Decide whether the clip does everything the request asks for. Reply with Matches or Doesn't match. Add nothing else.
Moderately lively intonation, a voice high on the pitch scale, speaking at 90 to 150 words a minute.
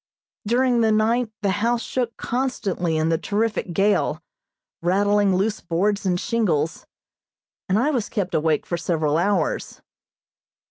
Matches